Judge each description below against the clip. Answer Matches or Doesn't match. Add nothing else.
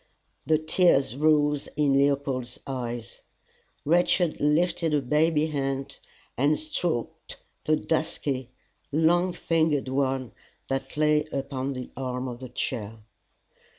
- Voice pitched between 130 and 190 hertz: Matches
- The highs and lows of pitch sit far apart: Doesn't match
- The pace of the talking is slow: Matches